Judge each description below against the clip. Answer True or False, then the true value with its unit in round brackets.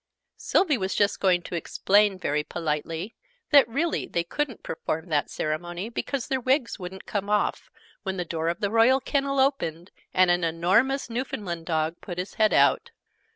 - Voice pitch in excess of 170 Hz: True (190 Hz)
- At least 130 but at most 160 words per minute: False (170 wpm)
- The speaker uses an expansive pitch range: True (6.1 semitones)